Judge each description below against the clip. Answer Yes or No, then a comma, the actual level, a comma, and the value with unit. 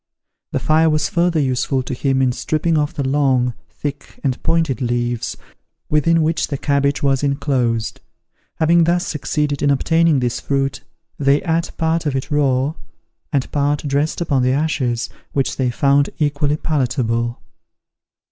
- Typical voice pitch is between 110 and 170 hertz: Yes, medium, 140 Hz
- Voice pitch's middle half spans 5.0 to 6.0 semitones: No, average, 2.8 semitones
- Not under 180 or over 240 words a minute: No, average, 150 wpm